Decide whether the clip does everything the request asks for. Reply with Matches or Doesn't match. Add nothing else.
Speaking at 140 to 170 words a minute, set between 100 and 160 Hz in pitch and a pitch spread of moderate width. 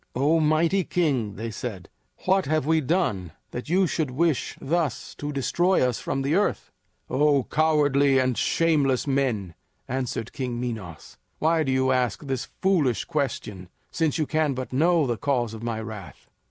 Matches